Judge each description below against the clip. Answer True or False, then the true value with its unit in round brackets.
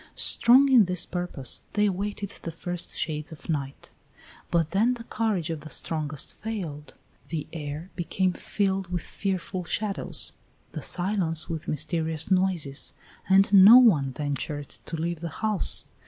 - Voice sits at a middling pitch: True (175 Hz)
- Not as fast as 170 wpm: True (145 wpm)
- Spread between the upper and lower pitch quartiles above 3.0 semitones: True (4.0 semitones)